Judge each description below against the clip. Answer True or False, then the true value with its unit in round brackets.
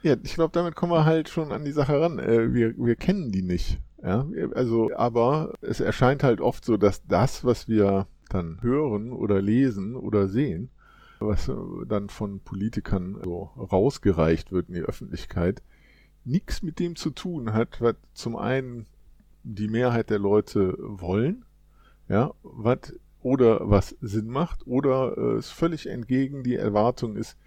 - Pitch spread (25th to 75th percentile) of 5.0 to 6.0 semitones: True (5.3 semitones)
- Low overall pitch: True (115 Hz)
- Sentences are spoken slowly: False (155 wpm)